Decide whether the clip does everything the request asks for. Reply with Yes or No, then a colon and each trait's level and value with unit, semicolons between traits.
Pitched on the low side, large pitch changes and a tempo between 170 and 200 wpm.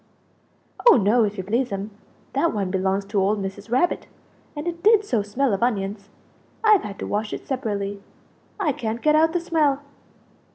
No: high, 220 Hz; wide, 6.9 semitones; average, 175 wpm